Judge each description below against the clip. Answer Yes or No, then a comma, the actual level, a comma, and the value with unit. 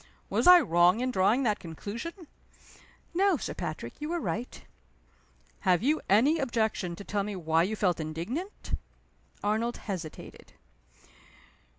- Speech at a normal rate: No, slow, 130 wpm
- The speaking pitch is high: Yes, high, 215 Hz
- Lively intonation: Yes, wide, 7.5 semitones